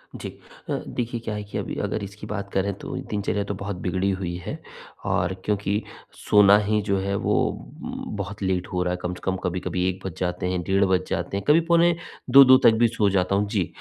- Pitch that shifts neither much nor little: No, narrow, 2.1 semitones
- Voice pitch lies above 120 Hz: No, low, 100 Hz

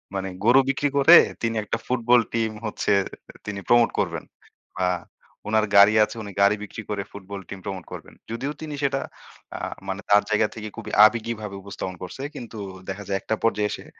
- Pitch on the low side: Yes, low, 110 Hz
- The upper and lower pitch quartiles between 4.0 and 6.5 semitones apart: No, average, 2.7 semitones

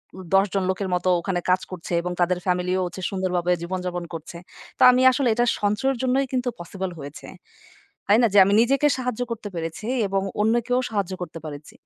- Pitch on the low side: No, high, 190 Hz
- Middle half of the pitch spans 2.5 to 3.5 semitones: No, average, 4.6 semitones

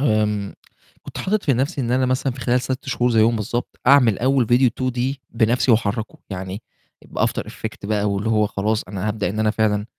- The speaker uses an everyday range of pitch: Yes, average, 3.3 semitones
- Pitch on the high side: No, low, 115 Hz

